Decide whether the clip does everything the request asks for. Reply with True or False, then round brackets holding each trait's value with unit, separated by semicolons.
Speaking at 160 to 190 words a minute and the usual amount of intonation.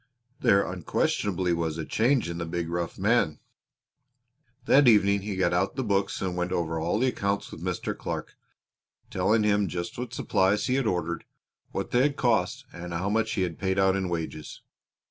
True (185 wpm; 3.6 semitones)